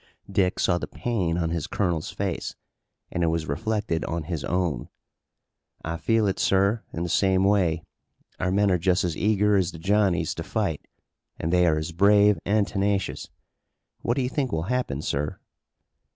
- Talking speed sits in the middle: Yes, average, 180 wpm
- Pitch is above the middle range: No, very low, 95 Hz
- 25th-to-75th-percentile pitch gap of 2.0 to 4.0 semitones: Yes, average, 3.7 semitones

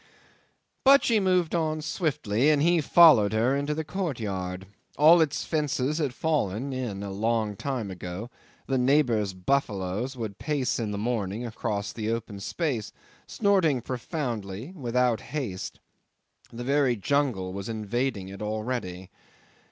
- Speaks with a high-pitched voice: No, low, 120 Hz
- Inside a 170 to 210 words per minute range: No, slow, 135 wpm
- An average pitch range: No, wide, 6.3 semitones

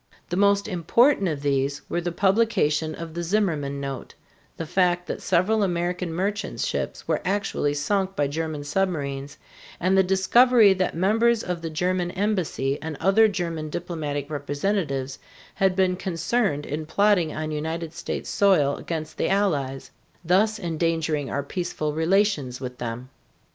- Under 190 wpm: Yes, average, 150 wpm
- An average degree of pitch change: Yes, average, 4.6 semitones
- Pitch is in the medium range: Yes, medium, 170 Hz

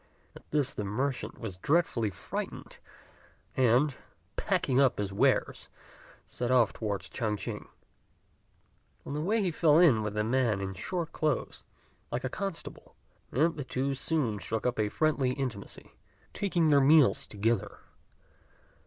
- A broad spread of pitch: Yes, wide, 5.8 semitones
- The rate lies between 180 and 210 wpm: No, average, 145 wpm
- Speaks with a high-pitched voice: No, low, 130 Hz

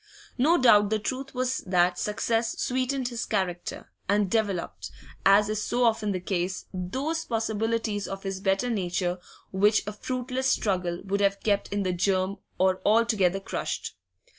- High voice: Yes, high, 205 Hz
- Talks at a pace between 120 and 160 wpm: Yes, average, 155 wpm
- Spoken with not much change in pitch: No, average, 3.5 semitones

